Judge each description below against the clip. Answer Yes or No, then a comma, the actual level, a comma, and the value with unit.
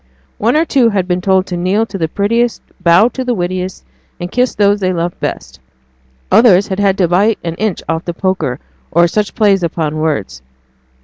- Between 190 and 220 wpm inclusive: Yes, average, 195 wpm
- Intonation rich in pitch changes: No, average, 3.5 semitones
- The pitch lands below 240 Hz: Yes, high, 190 Hz